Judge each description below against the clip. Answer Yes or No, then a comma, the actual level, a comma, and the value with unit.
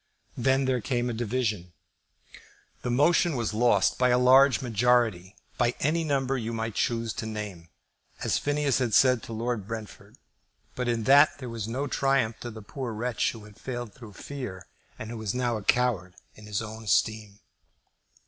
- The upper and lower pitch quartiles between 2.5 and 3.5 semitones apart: Yes, average, 2.8 semitones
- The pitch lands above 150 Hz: No, low, 120 Hz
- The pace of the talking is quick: No, average, 175 wpm